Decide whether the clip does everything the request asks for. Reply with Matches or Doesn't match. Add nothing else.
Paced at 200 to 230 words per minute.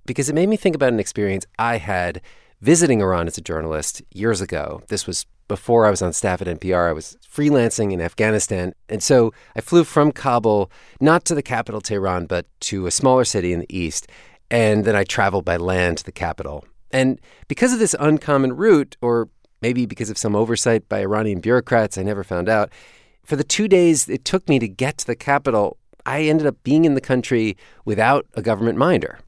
Matches